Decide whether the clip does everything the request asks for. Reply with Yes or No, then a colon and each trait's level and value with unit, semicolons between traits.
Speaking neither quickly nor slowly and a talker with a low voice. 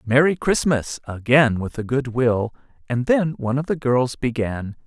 Yes: average, 175 wpm; low, 130 Hz